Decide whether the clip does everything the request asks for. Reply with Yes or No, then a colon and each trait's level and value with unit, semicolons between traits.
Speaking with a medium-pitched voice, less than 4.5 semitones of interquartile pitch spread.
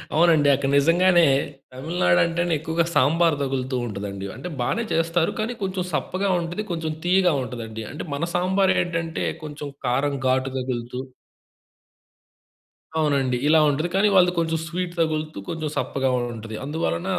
No: medium, 160 Hz; average, 4.8 semitones